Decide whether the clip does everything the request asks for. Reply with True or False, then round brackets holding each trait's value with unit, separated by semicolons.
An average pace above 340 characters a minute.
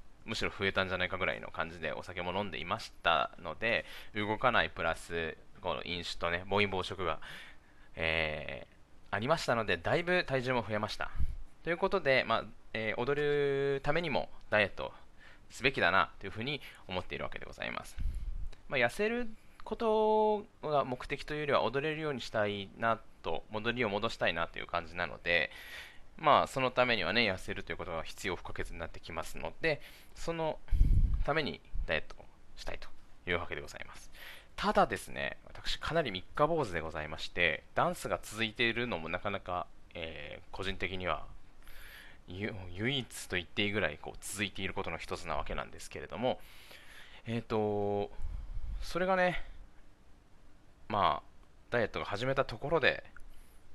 True (350 characters per minute)